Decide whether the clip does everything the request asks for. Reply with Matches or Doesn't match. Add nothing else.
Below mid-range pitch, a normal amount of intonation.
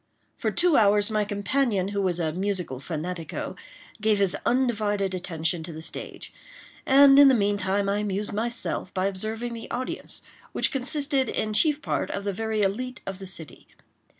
Doesn't match